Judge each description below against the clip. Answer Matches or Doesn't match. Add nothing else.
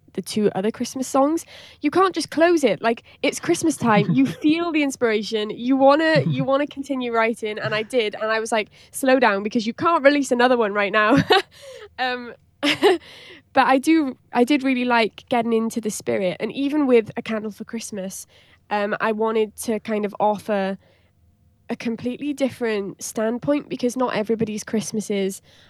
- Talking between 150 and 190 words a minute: Matches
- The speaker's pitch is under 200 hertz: Doesn't match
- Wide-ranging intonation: Doesn't match